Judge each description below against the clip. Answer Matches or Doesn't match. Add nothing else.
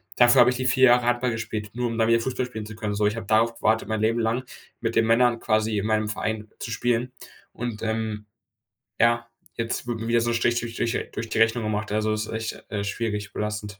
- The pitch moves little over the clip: Matches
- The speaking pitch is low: Matches